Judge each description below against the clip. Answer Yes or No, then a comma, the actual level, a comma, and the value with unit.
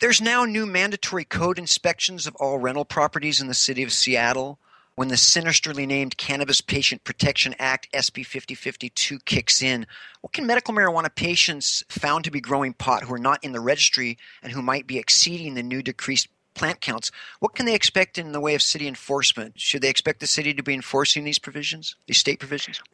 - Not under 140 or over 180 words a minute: No, average, 195 wpm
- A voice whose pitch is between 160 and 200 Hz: No, medium, 140 Hz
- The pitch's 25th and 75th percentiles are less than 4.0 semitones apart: No, average, 4.3 semitones